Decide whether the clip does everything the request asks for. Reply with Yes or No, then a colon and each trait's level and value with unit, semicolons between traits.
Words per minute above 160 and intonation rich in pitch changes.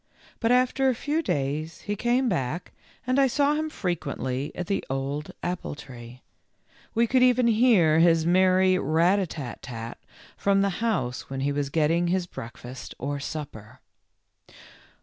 No: average, 155 wpm; wide, 8.3 semitones